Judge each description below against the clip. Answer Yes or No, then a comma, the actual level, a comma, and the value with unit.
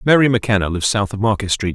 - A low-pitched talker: Yes, low, 105 Hz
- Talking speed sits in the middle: No, fast, 240 wpm